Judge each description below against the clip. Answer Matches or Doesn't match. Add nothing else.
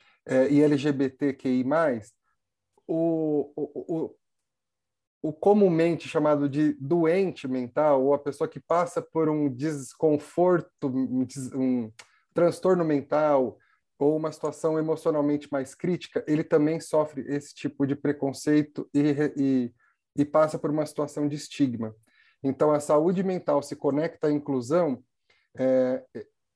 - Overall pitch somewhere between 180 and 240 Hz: Doesn't match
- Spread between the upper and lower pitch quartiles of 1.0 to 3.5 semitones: Matches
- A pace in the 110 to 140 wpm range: Matches